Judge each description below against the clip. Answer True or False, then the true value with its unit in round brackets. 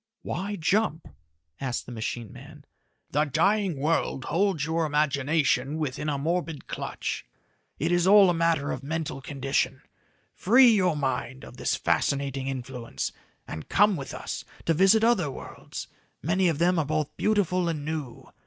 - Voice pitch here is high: False (155 Hz)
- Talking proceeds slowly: False (155 wpm)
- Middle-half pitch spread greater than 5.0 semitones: False (4.7 semitones)